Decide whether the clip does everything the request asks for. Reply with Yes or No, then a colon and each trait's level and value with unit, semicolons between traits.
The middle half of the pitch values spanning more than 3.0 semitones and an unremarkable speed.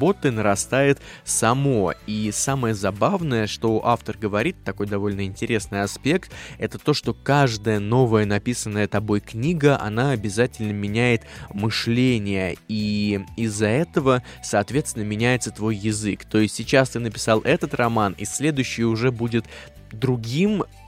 Yes: average, 3.4 semitones; average, 125 wpm